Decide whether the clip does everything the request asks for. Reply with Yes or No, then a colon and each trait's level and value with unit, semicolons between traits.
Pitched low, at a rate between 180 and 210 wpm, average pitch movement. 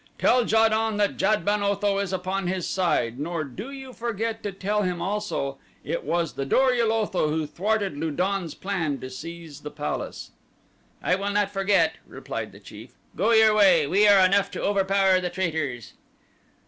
No: high, 195 Hz; average, 185 wpm; average, 3.9 semitones